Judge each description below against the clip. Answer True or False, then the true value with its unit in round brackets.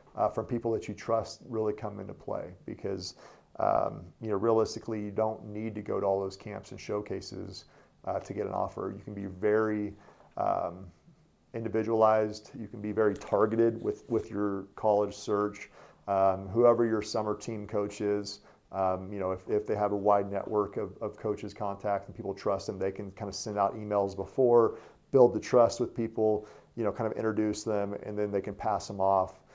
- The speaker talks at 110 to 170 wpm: False (200 wpm)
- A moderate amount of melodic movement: False (1.7 semitones)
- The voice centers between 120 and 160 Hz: False (105 Hz)